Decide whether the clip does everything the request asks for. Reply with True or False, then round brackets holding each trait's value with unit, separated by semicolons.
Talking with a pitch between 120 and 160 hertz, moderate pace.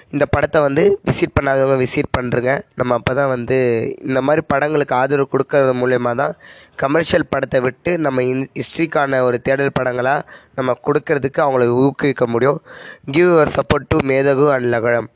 False (135 Hz; 155 wpm)